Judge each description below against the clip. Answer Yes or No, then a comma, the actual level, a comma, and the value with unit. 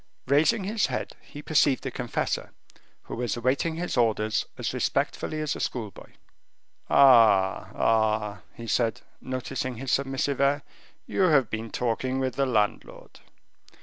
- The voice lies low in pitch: Yes, low, 130 Hz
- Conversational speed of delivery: Yes, average, 145 wpm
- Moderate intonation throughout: Yes, average, 3.8 semitones